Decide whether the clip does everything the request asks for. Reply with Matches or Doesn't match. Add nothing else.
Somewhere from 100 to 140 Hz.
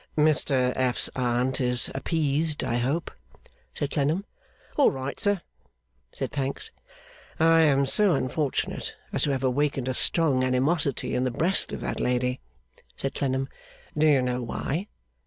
Matches